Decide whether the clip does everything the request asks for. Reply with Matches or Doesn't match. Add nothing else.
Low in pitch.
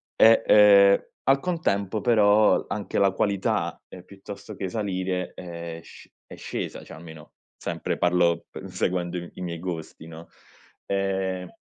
Matches